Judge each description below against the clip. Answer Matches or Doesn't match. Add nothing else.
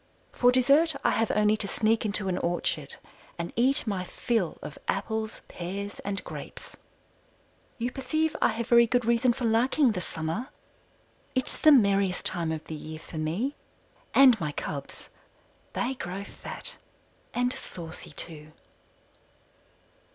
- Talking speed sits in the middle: Matches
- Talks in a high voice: Matches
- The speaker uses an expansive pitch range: Matches